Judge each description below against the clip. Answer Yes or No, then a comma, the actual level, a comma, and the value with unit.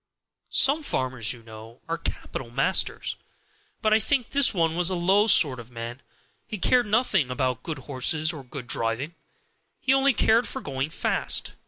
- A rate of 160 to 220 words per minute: Yes, average, 170 wpm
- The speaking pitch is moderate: Yes, medium, 155 Hz